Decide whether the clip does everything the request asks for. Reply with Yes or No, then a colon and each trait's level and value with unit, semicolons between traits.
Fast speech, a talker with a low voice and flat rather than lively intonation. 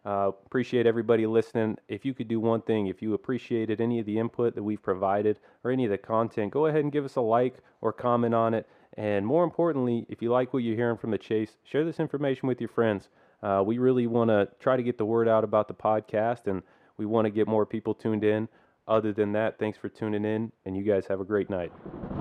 Yes: fast, 245 wpm; low, 110 Hz; narrow, 2.1 semitones